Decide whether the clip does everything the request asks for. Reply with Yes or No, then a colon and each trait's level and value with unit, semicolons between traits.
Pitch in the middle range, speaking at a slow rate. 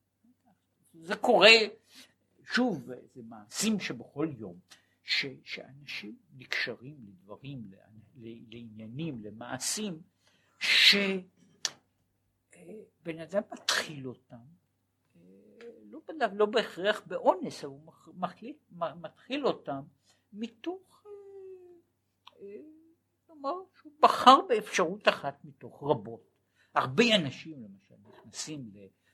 Yes: medium, 175 Hz; slow, 80 wpm